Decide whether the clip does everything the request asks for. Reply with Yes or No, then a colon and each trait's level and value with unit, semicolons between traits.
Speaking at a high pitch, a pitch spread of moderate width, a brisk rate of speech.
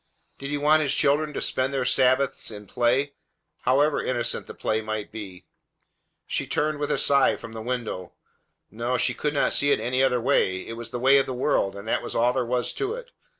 No: low, 125 Hz; average, 3.6 semitones; fast, 225 wpm